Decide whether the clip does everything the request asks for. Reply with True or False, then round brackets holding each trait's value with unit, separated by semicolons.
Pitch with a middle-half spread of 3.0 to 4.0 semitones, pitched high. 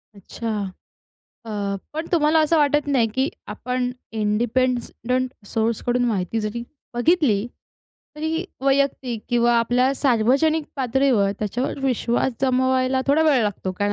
True (3.4 semitones; 250 Hz)